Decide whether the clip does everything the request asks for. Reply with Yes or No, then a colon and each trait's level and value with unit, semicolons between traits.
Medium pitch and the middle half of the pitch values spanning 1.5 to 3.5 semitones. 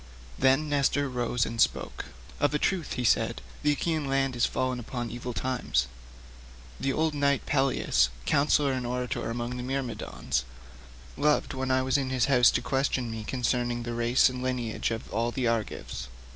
No: low, 125 Hz; narrow, 2.4 semitones